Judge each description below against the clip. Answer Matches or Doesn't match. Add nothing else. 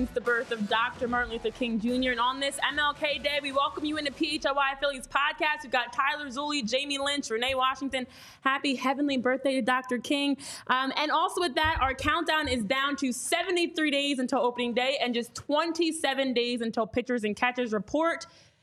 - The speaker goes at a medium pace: Matches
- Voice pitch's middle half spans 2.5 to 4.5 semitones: Matches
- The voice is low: Doesn't match